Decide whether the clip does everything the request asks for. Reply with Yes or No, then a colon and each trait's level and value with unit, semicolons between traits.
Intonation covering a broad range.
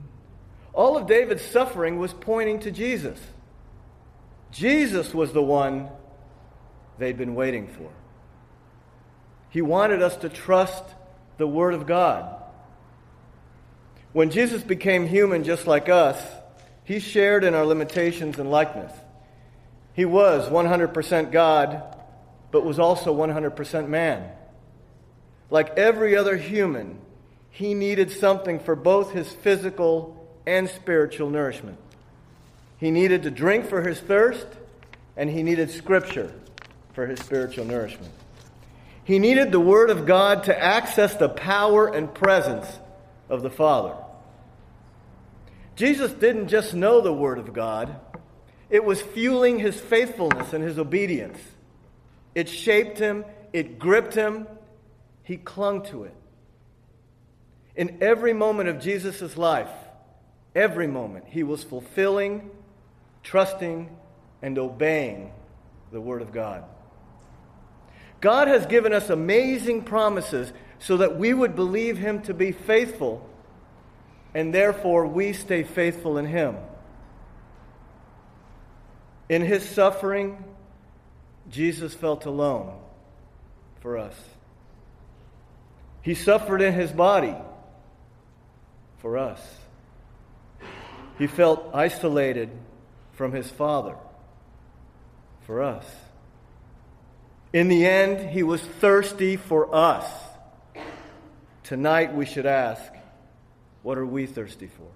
Yes: wide, 7.6 semitones